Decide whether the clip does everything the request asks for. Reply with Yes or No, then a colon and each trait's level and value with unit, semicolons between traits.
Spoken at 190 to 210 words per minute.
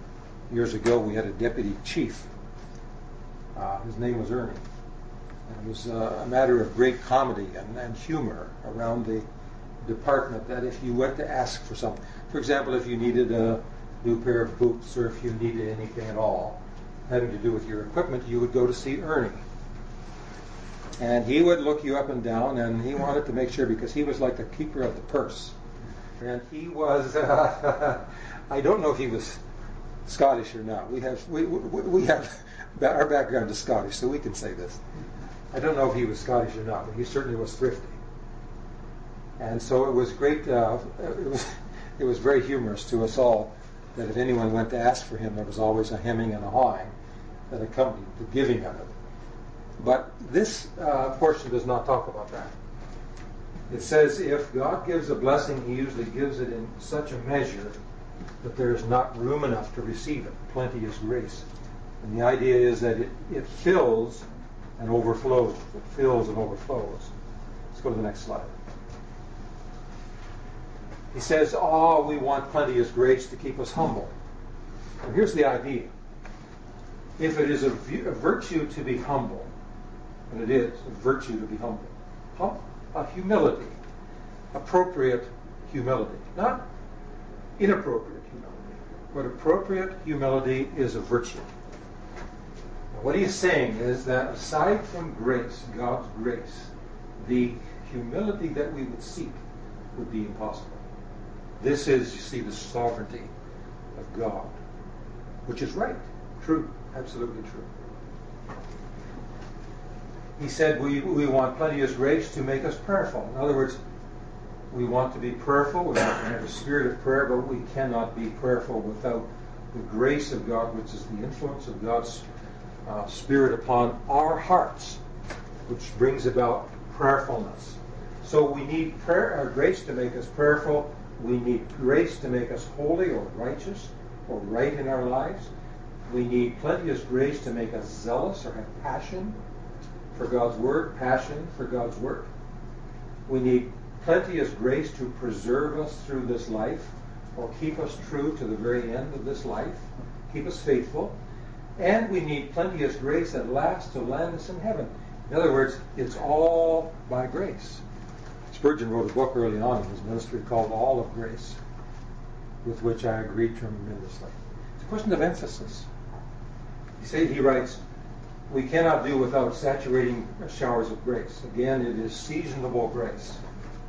No: average, 165 wpm